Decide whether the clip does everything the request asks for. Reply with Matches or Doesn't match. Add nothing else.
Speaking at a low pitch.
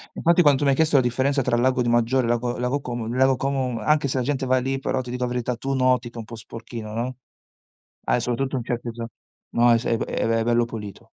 Matches